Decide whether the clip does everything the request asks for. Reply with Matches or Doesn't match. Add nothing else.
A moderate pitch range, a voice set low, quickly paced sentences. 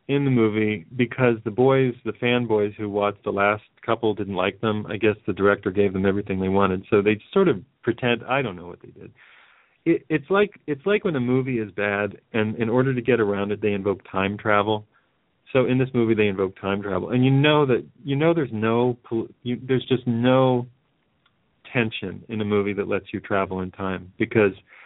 Matches